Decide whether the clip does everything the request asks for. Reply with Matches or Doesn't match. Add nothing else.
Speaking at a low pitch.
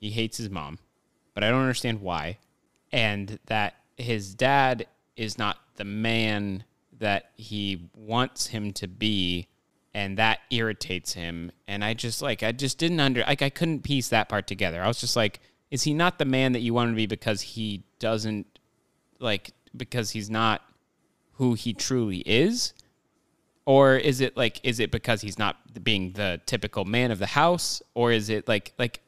Matches